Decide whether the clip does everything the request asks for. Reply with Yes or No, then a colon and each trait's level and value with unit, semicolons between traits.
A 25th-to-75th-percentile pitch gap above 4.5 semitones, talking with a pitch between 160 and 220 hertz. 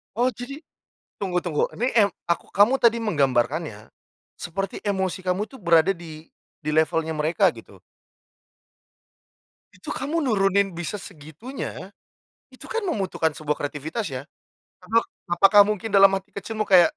Yes: average, 5.0 semitones; high, 190 Hz